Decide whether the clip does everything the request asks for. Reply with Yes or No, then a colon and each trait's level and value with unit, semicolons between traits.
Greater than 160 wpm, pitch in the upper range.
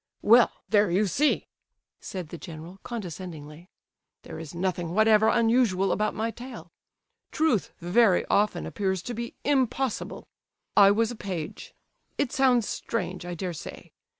No: slow, 135 wpm; high, 205 Hz